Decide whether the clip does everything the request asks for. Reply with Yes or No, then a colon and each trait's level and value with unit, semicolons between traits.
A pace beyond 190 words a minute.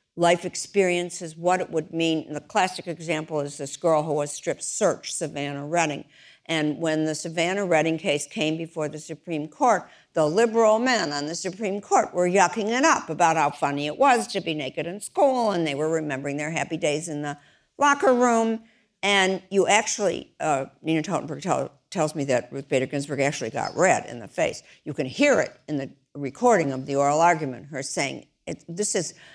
Yes: average, 200 wpm